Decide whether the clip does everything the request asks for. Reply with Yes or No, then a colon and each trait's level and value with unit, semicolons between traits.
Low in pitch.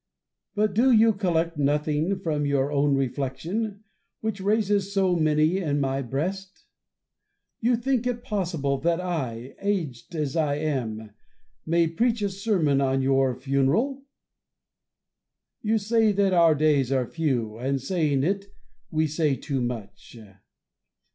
No: medium, 160 Hz